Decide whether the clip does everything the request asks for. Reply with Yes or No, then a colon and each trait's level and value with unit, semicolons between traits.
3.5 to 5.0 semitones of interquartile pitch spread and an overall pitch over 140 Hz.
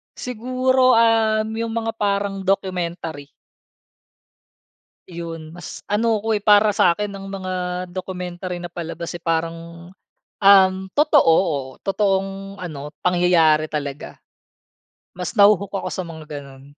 Yes: average, 3.8 semitones; high, 190 Hz